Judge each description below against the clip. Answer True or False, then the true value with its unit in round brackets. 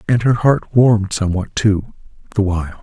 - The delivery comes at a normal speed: True (170 wpm)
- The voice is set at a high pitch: False (105 Hz)